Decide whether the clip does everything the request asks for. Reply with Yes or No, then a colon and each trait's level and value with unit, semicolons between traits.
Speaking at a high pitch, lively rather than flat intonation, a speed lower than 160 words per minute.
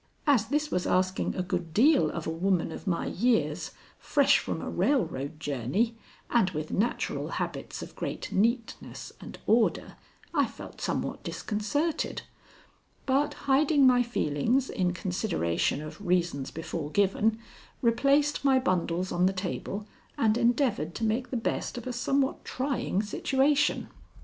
Yes: high, 215 Hz; wide, 6.5 semitones; average, 145 wpm